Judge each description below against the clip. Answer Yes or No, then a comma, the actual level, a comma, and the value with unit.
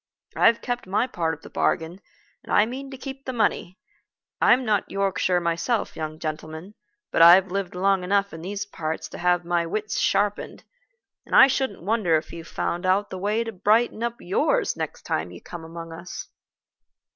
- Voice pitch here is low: No, high, 190 Hz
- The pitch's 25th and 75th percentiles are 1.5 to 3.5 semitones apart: No, average, 4.3 semitones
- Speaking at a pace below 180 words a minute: No, average, 185 wpm